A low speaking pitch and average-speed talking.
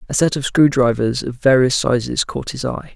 No: low, 130 Hz; fast, 225 wpm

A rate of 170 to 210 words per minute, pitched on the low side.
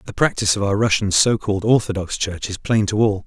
No: fast, 220 wpm; low, 105 Hz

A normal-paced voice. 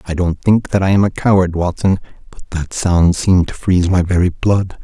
No: fast, 225 wpm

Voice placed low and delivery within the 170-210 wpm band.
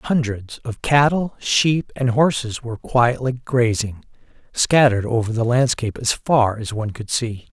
No: low, 120 Hz; average, 150 wpm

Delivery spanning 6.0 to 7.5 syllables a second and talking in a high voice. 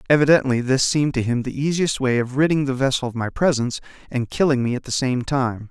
No: 6.1 syllables/s; low, 130 Hz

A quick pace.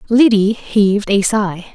No: average, 140 wpm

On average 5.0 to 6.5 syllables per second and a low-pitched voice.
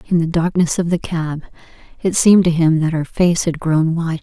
No: 5.4 syllables/s; medium, 165 Hz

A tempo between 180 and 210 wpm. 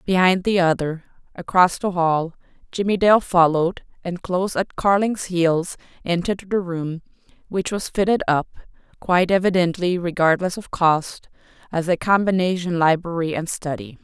No: slow, 135 wpm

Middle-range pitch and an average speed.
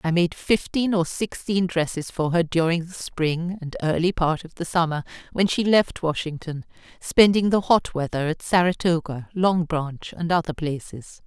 Yes: medium, 170 Hz; average, 170 wpm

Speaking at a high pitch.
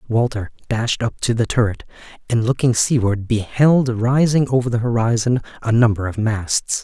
No: low, 115 Hz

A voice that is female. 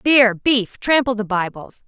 Yes: female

